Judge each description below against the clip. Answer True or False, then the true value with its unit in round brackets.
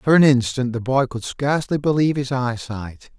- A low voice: True (130 Hz)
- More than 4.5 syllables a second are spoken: True (5.1 syllables/s)